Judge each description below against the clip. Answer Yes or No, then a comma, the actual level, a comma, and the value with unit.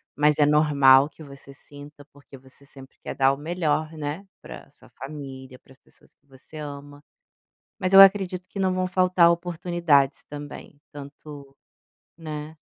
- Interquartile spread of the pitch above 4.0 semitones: No, average, 3.3 semitones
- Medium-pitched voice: Yes, medium, 150 Hz